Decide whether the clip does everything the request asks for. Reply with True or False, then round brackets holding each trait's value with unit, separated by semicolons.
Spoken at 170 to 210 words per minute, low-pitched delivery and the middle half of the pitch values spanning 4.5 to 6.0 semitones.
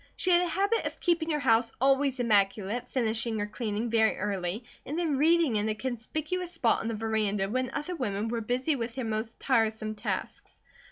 False (190 wpm; 235 Hz; 4.8 semitones)